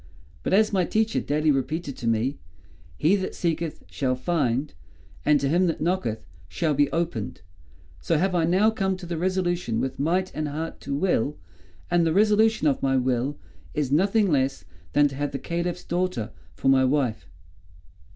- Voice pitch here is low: No, medium, 155 Hz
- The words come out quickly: No, average, 175 wpm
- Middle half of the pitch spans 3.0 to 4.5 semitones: No, average, 5.0 semitones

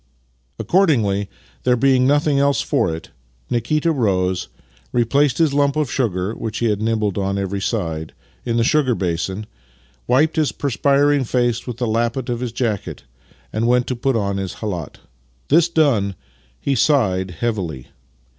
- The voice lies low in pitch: Yes, low, 120 Hz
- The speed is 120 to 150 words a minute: No, average, 160 wpm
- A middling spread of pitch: No, wide, 5.7 semitones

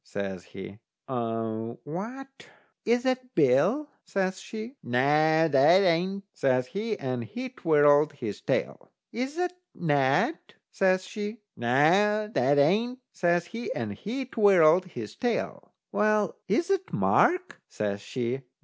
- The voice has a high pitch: No, medium, 175 Hz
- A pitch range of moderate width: No, wide, 8.9 semitones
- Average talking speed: No, slow, 125 wpm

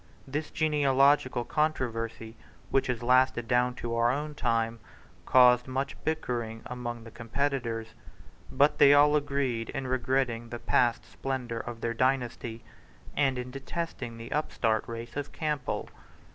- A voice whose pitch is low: Yes, low, 125 Hz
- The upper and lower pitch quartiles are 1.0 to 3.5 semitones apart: Yes, average, 3.0 semitones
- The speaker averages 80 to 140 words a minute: Yes, slow, 135 wpm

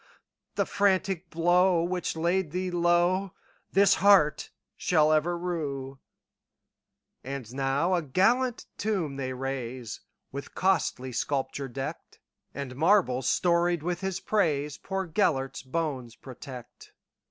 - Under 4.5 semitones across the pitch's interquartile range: No, average, 5.2 semitones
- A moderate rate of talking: No, slow, 95 wpm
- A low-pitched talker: No, medium, 165 Hz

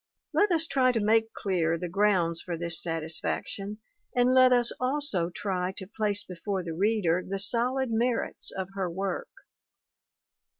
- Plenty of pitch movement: No, average, 5.0 semitones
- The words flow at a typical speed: Yes, average, 155 wpm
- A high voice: Yes, high, 200 Hz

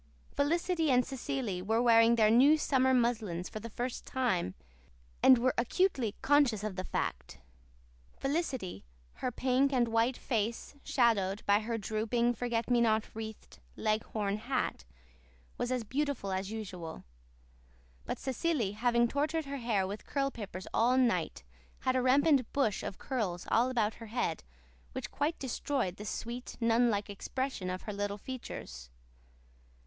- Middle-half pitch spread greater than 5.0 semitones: No, average, 3.9 semitones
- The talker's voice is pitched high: Yes, high, 235 Hz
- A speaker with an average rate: Yes, average, 150 wpm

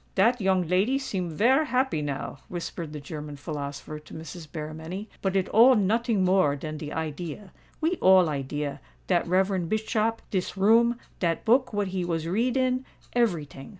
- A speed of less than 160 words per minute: Yes, average, 150 wpm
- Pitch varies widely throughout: Yes, wide, 6.4 semitones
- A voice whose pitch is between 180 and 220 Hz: Yes, medium, 185 Hz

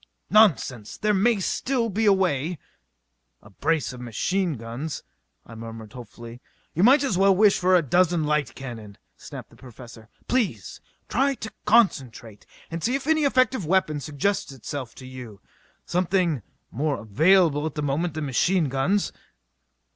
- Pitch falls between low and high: Yes, medium, 155 Hz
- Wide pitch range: Yes, wide, 7.8 semitones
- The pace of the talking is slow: No, average, 155 wpm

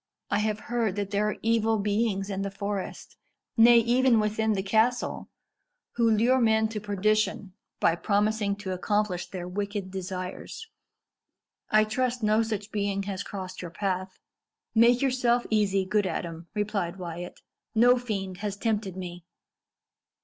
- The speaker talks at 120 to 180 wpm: Yes, average, 145 wpm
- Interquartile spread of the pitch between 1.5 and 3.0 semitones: Yes, narrow, 2.5 semitones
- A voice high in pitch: Yes, high, 205 Hz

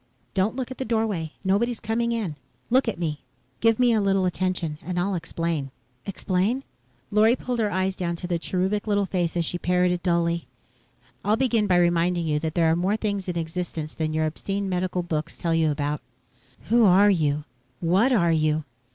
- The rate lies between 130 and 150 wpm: No, average, 190 wpm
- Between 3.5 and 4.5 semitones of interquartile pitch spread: Yes, average, 3.9 semitones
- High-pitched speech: No, medium, 180 Hz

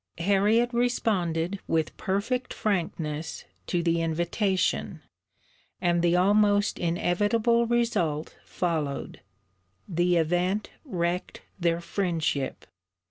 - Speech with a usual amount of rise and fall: Yes, average, 3.7 semitones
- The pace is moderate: No, slow, 85 wpm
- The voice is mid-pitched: Yes, medium, 180 Hz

